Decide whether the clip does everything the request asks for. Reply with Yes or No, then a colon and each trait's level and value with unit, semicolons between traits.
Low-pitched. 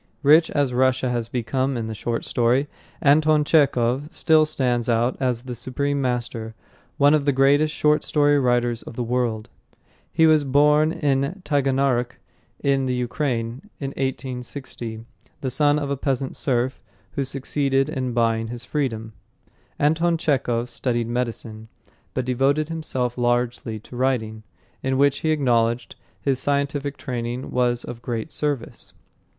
Yes: low, 130 Hz